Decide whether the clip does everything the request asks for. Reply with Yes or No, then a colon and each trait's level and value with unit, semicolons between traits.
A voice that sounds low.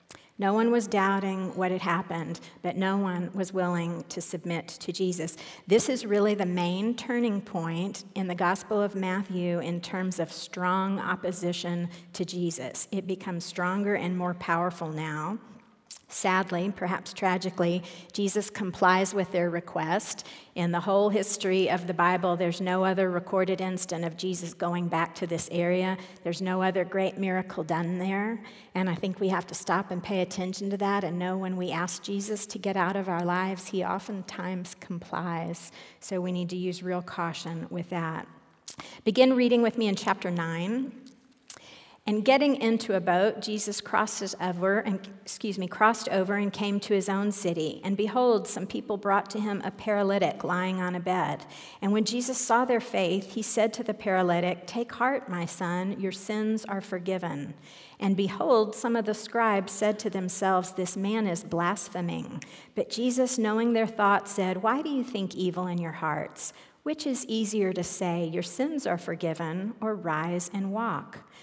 No: high, 190 Hz